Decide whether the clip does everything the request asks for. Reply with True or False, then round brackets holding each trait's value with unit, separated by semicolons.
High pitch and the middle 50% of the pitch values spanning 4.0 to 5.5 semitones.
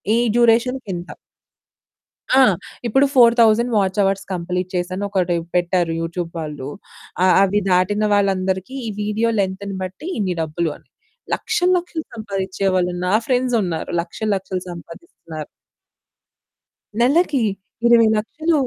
True (195 Hz; 4.5 semitones)